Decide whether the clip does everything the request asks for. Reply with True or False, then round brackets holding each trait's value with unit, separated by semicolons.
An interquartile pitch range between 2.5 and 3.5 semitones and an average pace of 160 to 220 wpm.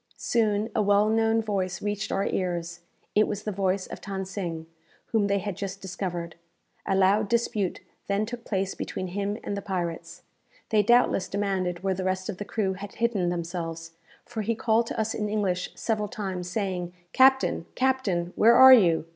True (2.9 semitones; 180 wpm)